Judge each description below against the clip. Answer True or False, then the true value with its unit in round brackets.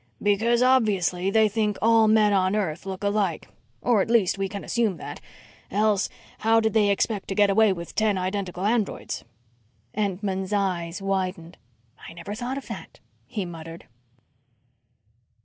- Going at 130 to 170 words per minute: True (150 wpm)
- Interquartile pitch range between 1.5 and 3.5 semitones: True (2.6 semitones)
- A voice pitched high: True (200 Hz)